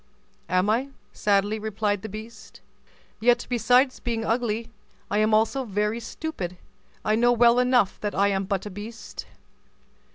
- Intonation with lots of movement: No, narrow, 2.6 semitones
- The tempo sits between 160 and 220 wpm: No, average, 150 wpm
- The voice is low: No, high, 220 Hz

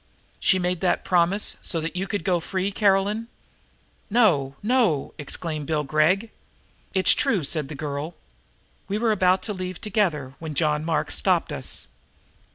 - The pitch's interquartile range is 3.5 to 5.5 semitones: Yes, average, 4.5 semitones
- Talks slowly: No, average, 155 wpm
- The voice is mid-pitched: Yes, medium, 180 Hz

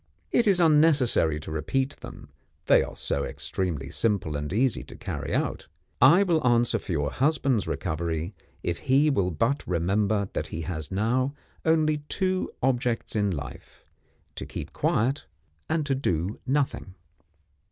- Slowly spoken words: No, average, 150 wpm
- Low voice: Yes, low, 115 Hz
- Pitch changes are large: Yes, wide, 8.5 semitones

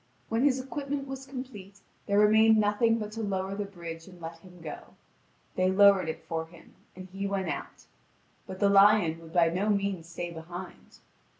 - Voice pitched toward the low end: No, high, 195 Hz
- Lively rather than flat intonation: No, average, 3.6 semitones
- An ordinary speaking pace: Yes, average, 185 wpm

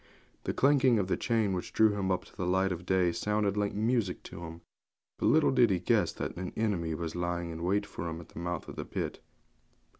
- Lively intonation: No, average, 3.5 semitones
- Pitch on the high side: No, very low, 95 Hz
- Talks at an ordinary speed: No, fast, 235 wpm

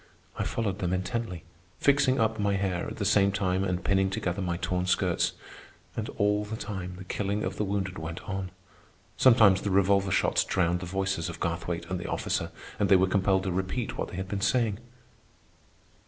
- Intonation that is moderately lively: No, narrow, 2.1 semitones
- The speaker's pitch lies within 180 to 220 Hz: No, very low, 95 Hz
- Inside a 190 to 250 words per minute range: Yes, average, 195 wpm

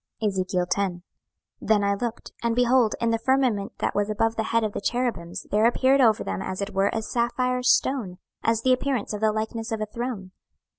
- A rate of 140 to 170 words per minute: No, average, 200 wpm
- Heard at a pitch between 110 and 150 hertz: No, high, 220 Hz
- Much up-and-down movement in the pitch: No, average, 3.3 semitones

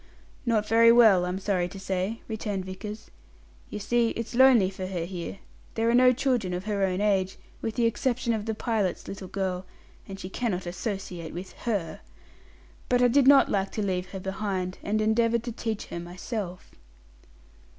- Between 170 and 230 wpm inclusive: Yes, average, 180 wpm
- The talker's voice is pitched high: Yes, high, 205 Hz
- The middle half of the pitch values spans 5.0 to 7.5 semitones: No, average, 3.7 semitones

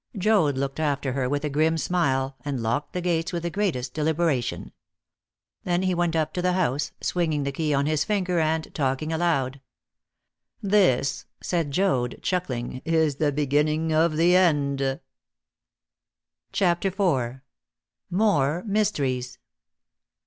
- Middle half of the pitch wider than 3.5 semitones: Yes, average, 4.2 semitones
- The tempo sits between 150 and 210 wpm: No, slow, 135 wpm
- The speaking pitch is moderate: Yes, medium, 155 Hz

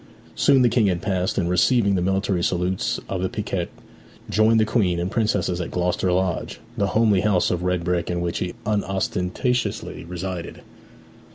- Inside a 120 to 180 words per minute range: Yes, average, 170 wpm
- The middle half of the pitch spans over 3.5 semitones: No, average, 2.9 semitones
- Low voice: Yes, very low, 95 Hz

